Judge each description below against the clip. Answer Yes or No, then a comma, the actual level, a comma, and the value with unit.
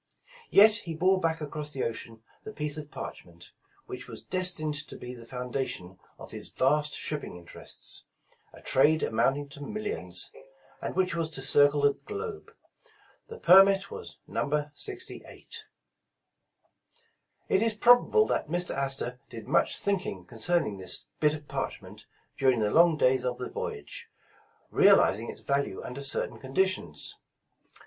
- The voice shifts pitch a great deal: Yes, wide, 6.5 semitones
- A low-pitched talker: No, medium, 150 Hz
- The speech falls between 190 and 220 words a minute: No, average, 150 wpm